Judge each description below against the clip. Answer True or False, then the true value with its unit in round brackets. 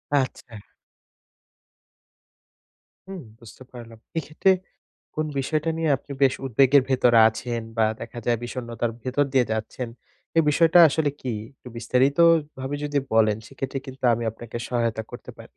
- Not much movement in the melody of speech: False (3.3 semitones)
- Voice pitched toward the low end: True (130 Hz)